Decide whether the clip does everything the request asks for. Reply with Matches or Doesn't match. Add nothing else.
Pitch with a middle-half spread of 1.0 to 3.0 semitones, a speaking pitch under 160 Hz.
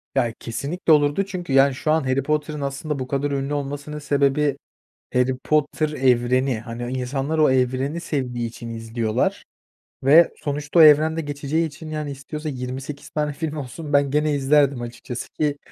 Matches